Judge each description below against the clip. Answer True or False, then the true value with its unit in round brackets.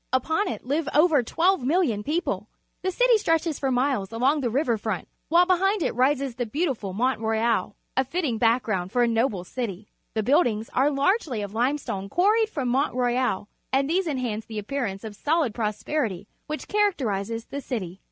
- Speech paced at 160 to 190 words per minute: True (180 wpm)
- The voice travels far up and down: True (5.8 semitones)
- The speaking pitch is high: True (255 Hz)